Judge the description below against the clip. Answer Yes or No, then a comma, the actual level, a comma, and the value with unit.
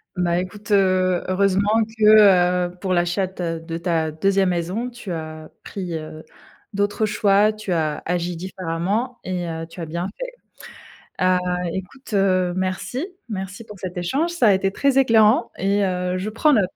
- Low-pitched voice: No, medium, 185 Hz